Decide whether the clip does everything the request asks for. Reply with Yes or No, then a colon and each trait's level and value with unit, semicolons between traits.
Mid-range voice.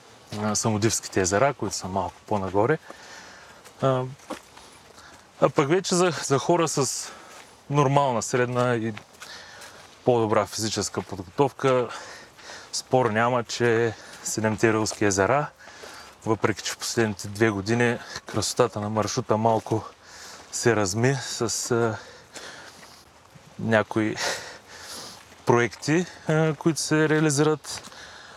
No: low, 115 Hz